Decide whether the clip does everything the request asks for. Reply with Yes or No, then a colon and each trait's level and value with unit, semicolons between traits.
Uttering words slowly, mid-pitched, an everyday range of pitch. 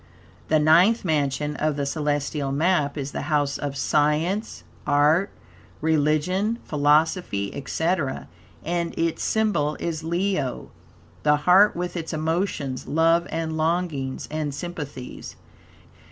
Yes: slow, 115 wpm; medium, 155 Hz; average, 3.0 semitones